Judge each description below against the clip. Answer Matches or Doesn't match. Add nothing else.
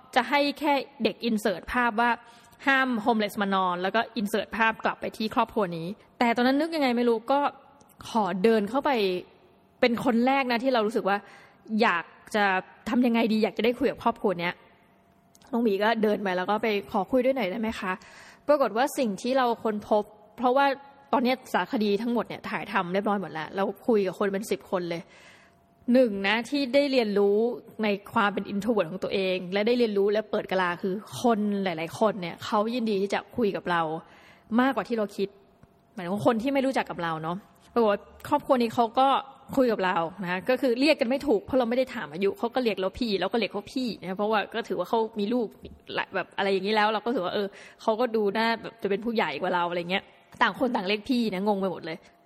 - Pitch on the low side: Doesn't match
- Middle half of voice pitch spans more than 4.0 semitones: Doesn't match